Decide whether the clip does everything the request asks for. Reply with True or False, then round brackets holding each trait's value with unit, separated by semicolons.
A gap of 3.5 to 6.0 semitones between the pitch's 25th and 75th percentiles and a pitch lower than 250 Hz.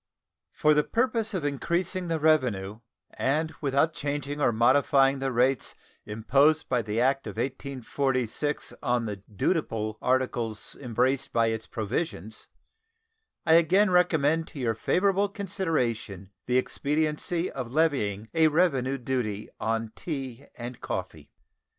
True (5.5 semitones; 135 Hz)